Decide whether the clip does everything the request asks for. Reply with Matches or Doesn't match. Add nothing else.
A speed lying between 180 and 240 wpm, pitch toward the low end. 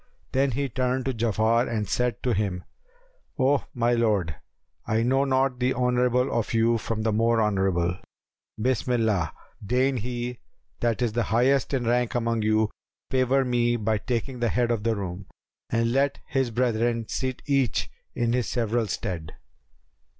Doesn't match